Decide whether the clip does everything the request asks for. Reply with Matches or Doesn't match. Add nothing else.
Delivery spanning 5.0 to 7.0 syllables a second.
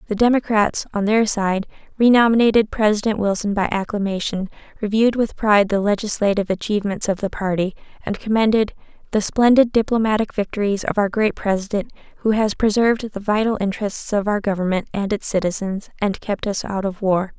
Matches